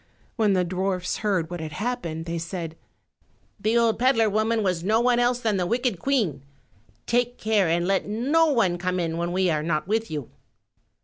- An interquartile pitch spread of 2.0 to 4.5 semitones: No, average, 5.1 semitones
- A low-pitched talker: No, high, 195 Hz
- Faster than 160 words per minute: Yes, average, 190 wpm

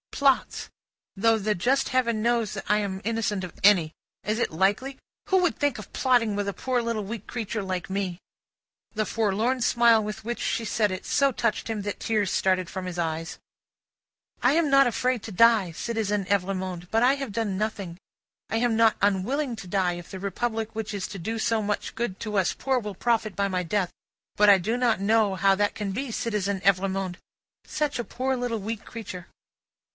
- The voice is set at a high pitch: Yes, high, 215 Hz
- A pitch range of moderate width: Yes, average, 3.3 semitones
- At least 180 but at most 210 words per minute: Yes, average, 200 wpm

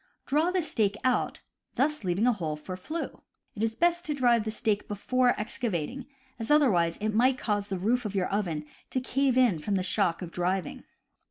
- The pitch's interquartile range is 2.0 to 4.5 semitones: No, average, 5.3 semitones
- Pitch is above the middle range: Yes, high, 220 Hz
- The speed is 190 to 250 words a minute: Yes, average, 195 wpm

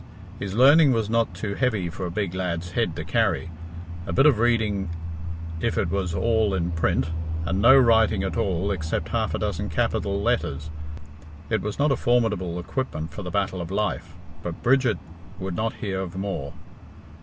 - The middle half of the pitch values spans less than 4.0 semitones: No, average, 4.5 semitones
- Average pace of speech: Yes, average, 180 wpm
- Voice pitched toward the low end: Yes, low, 100 Hz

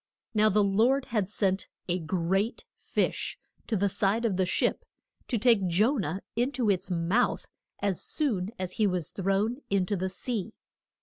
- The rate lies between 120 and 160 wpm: No, average, 175 wpm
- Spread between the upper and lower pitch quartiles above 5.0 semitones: No, average, 3.5 semitones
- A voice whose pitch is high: Yes, high, 200 Hz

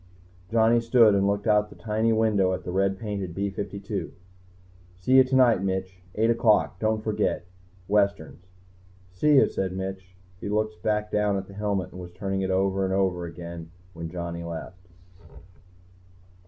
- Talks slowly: No, average, 165 wpm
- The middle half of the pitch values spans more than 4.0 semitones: No, narrow, 2.6 semitones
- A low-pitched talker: Yes, low, 100 Hz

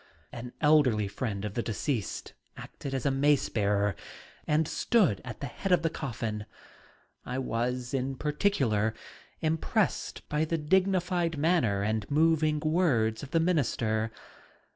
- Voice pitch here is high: No, medium, 140 Hz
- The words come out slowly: Yes, slow, 130 wpm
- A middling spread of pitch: No, wide, 6.3 semitones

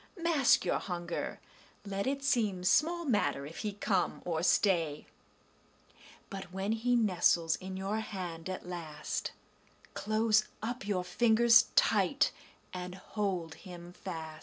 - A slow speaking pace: Yes, slow, 130 wpm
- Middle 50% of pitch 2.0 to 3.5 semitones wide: No, average, 4.0 semitones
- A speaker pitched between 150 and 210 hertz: Yes, high, 190 Hz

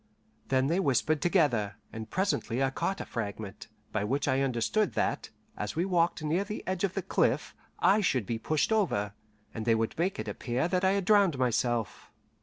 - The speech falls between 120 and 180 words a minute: No, average, 195 wpm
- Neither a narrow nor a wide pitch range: No, wide, 8.4 semitones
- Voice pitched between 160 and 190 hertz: No, low, 135 Hz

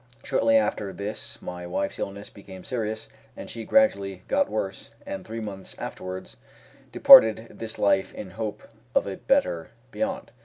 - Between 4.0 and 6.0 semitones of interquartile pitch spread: No, average, 2.8 semitones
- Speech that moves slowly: No, average, 150 wpm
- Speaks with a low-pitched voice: Yes, low, 105 Hz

